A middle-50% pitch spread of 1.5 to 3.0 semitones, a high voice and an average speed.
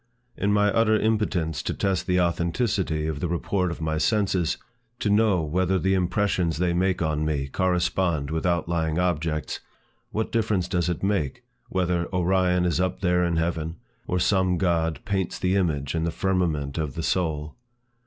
No: average, 2.7 semitones; very low, 90 Hz; average, 170 wpm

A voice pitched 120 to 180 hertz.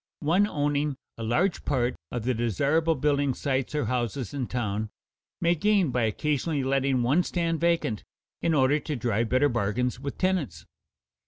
Yes: low, 135 Hz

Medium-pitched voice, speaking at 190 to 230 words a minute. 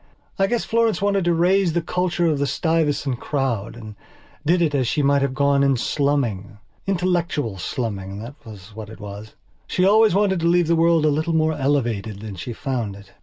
Yes: medium, 145 Hz; average, 200 wpm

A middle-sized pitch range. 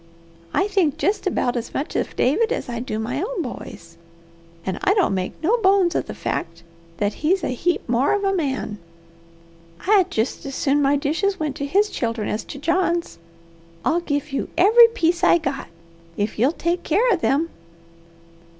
No: wide, 7.0 semitones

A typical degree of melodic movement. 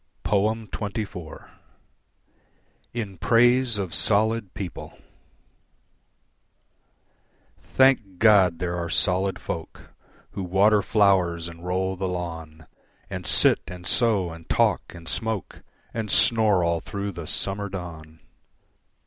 Yes: average, 3.6 semitones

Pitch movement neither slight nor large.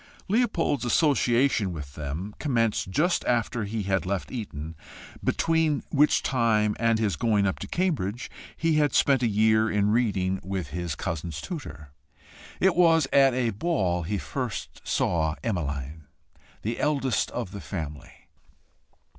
No: wide, 6.6 semitones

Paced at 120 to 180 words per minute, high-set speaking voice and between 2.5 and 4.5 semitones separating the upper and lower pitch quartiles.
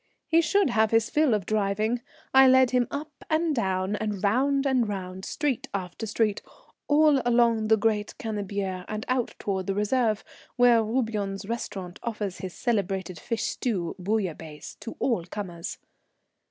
Yes: average, 155 wpm; high, 215 Hz; average, 4.0 semitones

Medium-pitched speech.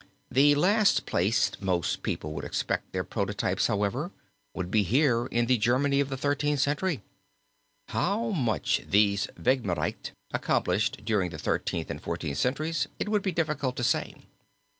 No: low, 130 Hz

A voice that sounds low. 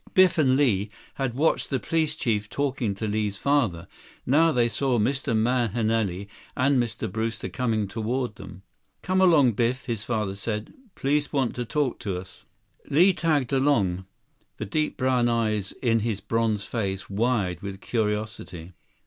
Yes: low, 115 Hz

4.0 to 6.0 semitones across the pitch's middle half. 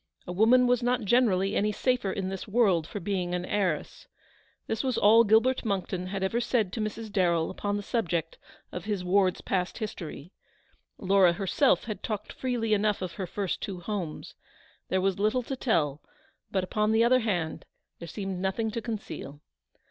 No: average, 3.5 semitones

